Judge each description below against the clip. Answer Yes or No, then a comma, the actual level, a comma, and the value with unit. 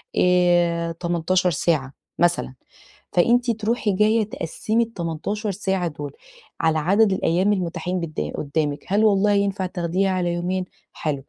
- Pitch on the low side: No, medium, 180 Hz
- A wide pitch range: No, average, 3.3 semitones